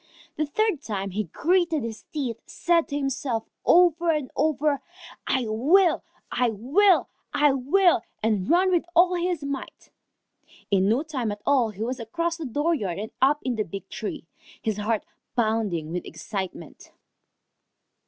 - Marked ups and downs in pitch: Yes, wide, 7.2 semitones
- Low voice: No, very high, 265 Hz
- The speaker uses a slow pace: No, average, 155 wpm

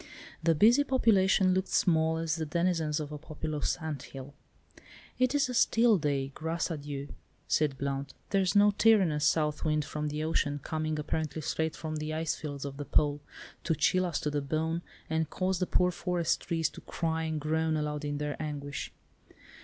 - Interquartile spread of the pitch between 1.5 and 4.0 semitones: Yes, average, 2.7 semitones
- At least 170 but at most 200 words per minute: Yes, average, 180 wpm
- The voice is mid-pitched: Yes, medium, 155 Hz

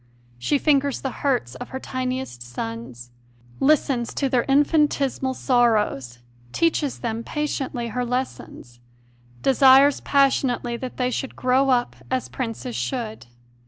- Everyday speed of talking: No, slow, 125 wpm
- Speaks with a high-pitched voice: Yes, very high, 255 Hz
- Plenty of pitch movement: No, average, 2.8 semitones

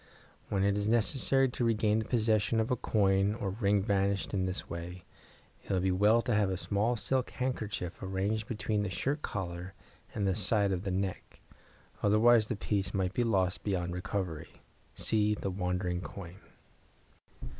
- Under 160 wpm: No, average, 165 wpm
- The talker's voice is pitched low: Yes, low, 100 Hz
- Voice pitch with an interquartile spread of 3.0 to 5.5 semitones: No, narrow, 2.6 semitones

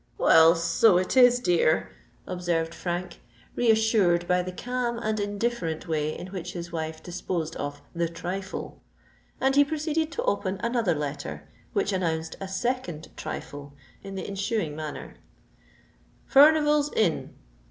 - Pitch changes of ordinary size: No, wide, 6.0 semitones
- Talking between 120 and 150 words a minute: Yes, slow, 135 wpm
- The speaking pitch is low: No, medium, 185 Hz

